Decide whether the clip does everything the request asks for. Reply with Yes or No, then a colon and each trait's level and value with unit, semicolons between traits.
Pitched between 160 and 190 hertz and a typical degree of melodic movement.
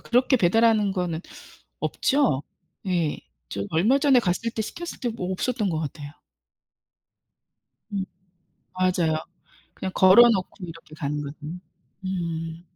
No: medium, 185 Hz; wide, 5.7 semitones